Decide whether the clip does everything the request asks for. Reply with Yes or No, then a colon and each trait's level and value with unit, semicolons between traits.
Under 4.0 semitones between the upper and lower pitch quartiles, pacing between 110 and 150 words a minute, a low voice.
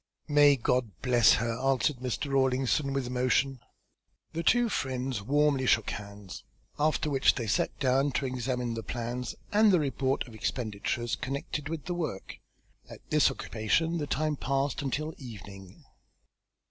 Yes: average, 3.5 semitones; average, 145 wpm; low, 130 Hz